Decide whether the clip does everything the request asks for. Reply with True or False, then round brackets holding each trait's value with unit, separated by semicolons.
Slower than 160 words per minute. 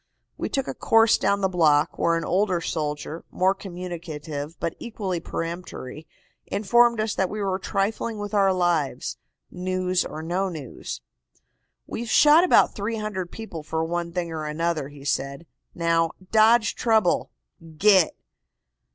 True (145 wpm)